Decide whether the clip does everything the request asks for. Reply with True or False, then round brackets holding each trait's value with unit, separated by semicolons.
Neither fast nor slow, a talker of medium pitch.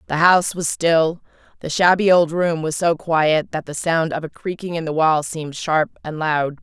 False (215 wpm; 165 Hz)